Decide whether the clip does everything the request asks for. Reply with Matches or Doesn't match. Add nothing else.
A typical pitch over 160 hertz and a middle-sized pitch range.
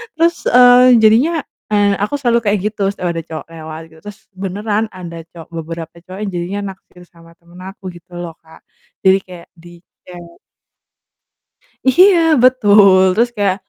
Matches